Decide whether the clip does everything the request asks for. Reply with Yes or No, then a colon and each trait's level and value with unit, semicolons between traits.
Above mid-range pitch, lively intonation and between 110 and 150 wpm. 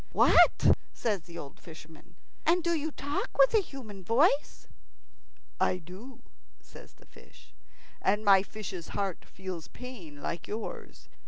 Yes: high, 205 Hz; wide, 7.3 semitones; average, 140 wpm